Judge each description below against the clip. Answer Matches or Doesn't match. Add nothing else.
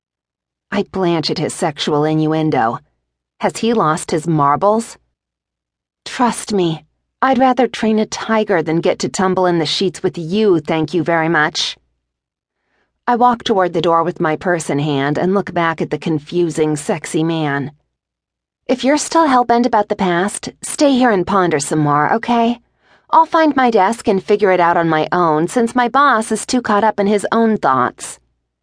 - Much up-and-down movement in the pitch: Matches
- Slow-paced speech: Doesn't match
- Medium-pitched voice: Matches